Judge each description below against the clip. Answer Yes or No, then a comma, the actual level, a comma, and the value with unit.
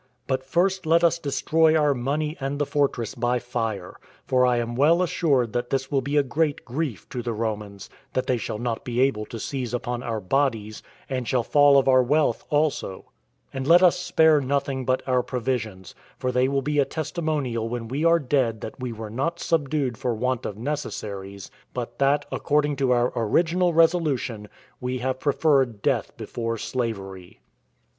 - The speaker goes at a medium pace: Yes, average, 180 wpm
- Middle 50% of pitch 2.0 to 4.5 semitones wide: Yes, average, 3.9 semitones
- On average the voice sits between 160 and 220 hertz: No, low, 130 Hz